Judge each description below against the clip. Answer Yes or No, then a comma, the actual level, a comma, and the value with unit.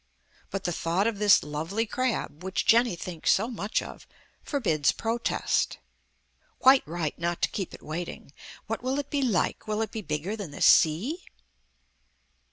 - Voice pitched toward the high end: Yes, high, 200 Hz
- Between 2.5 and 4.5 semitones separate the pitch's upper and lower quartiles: No, wide, 5.5 semitones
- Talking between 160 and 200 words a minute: Yes, average, 165 wpm